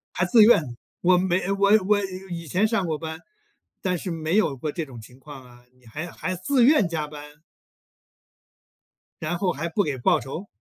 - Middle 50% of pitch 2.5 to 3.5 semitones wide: No, average, 4.4 semitones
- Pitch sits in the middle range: Yes, medium, 170 Hz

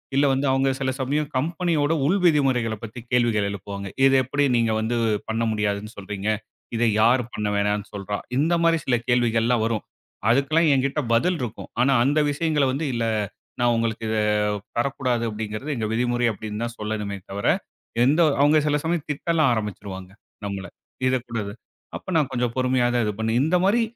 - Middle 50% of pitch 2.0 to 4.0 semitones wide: No, average, 4.5 semitones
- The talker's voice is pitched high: No, low, 120 Hz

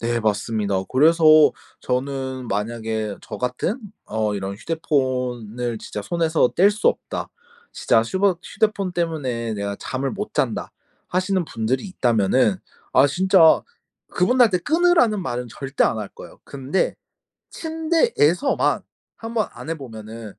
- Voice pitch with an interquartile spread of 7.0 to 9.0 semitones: Yes, wide, 8.3 semitones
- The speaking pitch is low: Yes, low, 130 Hz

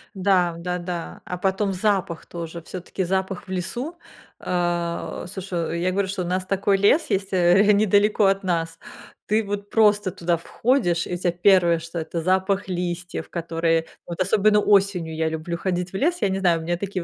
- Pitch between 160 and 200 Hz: Yes, medium, 185 Hz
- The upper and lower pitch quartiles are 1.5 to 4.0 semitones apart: Yes, narrow, 2.5 semitones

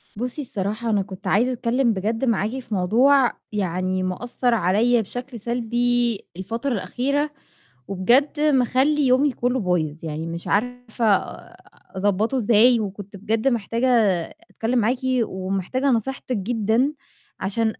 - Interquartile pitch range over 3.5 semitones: Yes, average, 4.0 semitones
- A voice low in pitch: No, high, 230 Hz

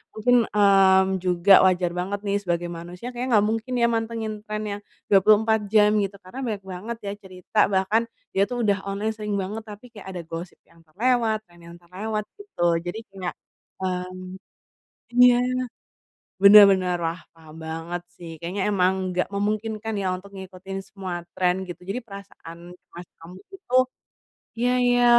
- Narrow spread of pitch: No, average, 3.2 semitones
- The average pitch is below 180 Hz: No, high, 195 Hz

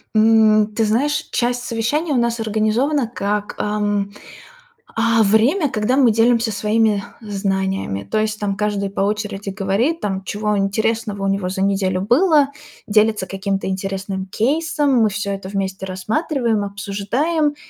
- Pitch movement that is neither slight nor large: Yes, average, 3.1 semitones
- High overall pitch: Yes, high, 210 Hz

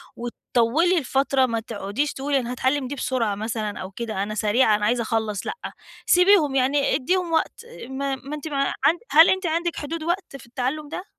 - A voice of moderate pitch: No, very high, 270 Hz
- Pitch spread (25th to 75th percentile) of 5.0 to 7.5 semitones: Yes, average, 5.3 semitones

